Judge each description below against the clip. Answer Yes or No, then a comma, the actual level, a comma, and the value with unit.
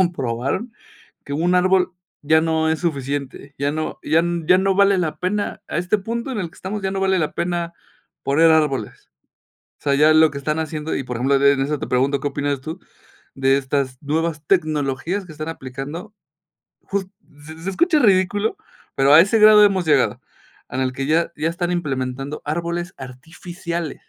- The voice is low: No, medium, 160 Hz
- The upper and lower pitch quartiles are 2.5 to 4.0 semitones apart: No, average, 4.6 semitones